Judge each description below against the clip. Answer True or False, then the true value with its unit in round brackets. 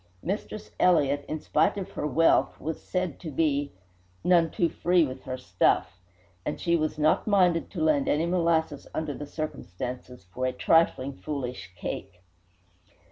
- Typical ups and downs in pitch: True (4.6 semitones)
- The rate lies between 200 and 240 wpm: False (155 wpm)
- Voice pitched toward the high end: False (150 Hz)